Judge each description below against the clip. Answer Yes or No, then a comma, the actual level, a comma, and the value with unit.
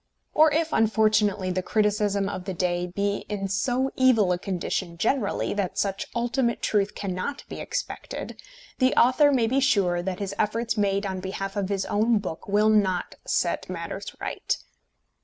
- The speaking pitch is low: No, high, 205 Hz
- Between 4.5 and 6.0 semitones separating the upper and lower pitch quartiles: No, average, 3.5 semitones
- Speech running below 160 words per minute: No, average, 165 wpm